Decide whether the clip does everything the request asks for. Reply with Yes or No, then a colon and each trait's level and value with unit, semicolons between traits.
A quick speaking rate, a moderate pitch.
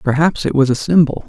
Yes: fast, 235 wpm; medium, 145 Hz